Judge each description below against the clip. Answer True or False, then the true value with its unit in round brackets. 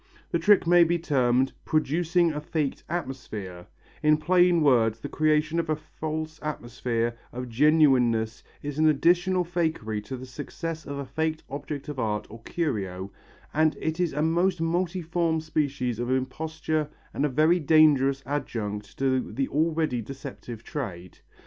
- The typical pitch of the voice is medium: True (150 Hz)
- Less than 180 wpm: True (150 wpm)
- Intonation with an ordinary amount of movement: True (4.3 semitones)